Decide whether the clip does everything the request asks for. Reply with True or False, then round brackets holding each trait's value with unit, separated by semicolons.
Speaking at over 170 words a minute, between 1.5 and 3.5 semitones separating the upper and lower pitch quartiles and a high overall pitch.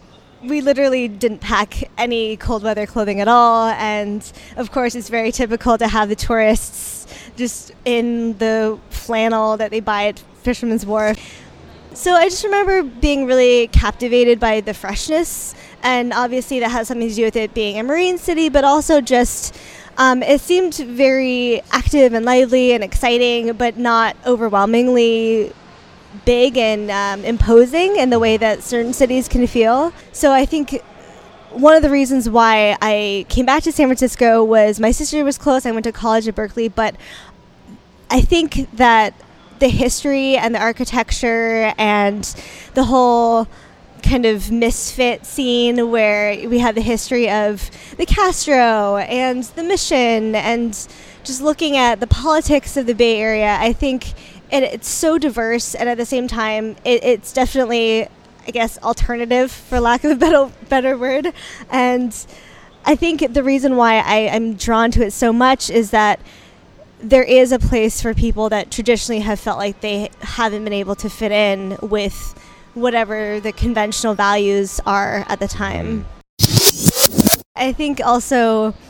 False (160 wpm; 2.9 semitones; 235 Hz)